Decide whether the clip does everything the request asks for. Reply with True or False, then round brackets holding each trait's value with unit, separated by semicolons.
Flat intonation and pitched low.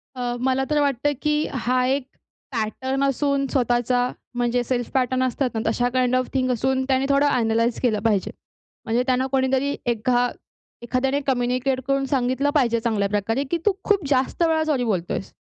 False (2.1 semitones; 255 Hz)